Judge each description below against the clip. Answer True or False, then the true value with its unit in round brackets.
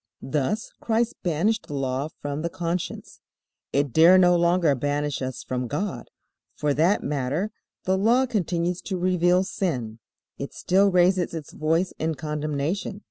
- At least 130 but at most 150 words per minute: True (145 wpm)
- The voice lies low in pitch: False (170 Hz)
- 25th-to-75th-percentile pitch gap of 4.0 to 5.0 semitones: True (4.3 semitones)